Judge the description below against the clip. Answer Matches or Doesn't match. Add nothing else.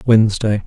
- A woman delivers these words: Doesn't match